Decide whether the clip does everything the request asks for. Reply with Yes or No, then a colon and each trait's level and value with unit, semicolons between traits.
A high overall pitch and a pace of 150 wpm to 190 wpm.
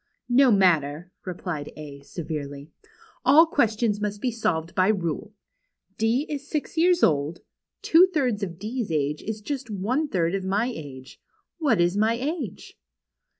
Yes: high, 205 Hz; average, 155 wpm